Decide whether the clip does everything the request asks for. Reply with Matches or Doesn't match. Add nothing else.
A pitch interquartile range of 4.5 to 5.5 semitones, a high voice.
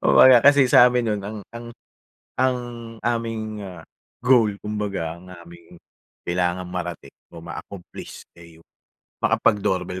Doesn't match